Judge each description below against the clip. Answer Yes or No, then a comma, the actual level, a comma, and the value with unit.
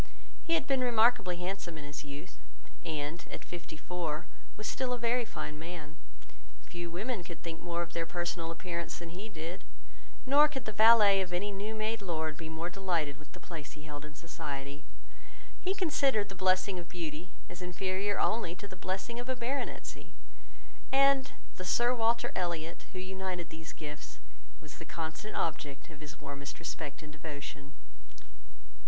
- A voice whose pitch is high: No, medium, 175 Hz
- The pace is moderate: Yes, average, 170 wpm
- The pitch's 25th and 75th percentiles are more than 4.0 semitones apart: Yes, average, 5.2 semitones